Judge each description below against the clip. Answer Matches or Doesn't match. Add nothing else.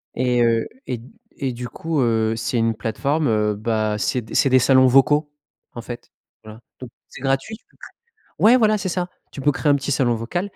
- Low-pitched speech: Matches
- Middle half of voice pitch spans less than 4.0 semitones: Doesn't match